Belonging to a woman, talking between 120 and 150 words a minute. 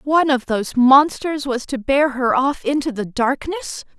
No: female; average, 180 wpm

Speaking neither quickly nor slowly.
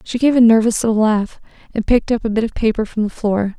No: fast, 265 wpm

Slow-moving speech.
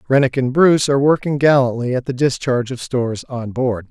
No: average, 200 wpm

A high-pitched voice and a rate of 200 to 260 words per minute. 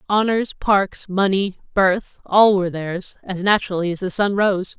No: high, 195 Hz; average, 150 wpm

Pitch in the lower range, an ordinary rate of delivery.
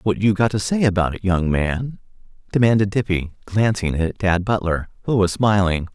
Yes: low, 100 Hz; average, 180 wpm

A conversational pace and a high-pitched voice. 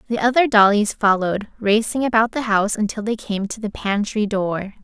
Yes: average, 185 wpm; high, 215 Hz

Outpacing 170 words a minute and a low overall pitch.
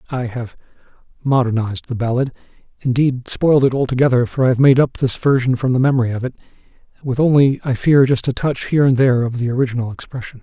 Yes: average, 190 wpm; low, 130 Hz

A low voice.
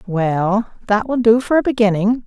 No: high, 220 Hz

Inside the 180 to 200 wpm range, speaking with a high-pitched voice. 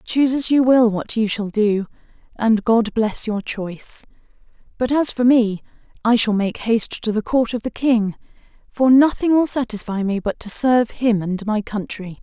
Yes: average, 190 wpm; high, 225 Hz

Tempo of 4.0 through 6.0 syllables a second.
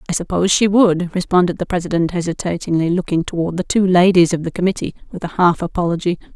No: 6.5 syllables/s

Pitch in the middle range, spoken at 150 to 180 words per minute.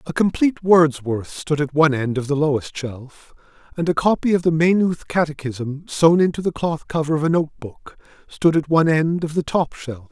No: medium, 155 Hz; average, 200 wpm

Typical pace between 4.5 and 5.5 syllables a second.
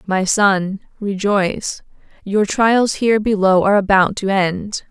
No: 4.1 syllables/s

